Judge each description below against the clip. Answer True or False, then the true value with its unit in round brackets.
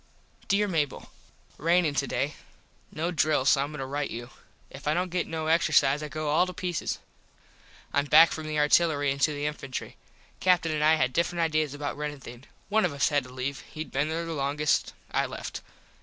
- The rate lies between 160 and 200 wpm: True (195 wpm)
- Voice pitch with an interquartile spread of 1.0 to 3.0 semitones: True (2.5 semitones)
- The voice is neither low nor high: True (150 Hz)